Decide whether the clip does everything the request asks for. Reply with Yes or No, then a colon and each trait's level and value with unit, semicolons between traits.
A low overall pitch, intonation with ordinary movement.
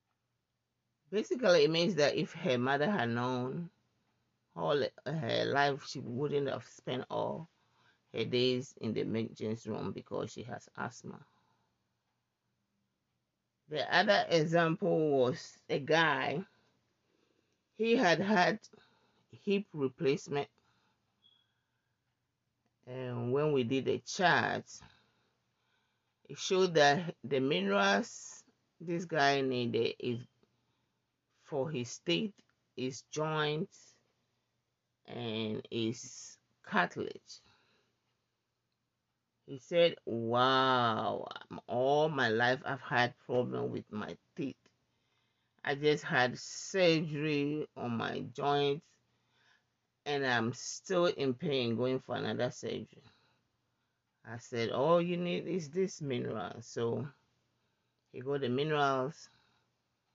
Yes: low, 130 Hz; average, 4.0 semitones